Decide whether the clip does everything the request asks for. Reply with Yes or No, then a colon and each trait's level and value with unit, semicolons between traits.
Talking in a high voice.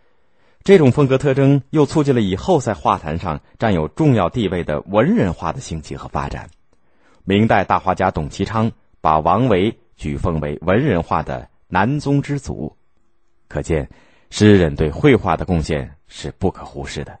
No: very low, 95 Hz